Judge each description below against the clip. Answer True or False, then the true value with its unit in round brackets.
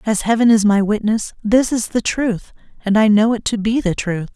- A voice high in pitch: True (215 Hz)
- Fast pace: True (235 wpm)